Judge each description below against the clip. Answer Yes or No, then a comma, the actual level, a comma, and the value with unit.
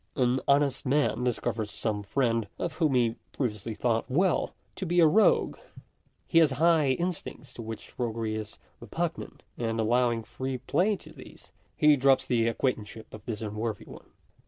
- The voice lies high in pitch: No, low, 125 Hz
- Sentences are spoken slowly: No, average, 175 wpm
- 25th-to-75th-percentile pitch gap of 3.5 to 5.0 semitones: Yes, average, 4.5 semitones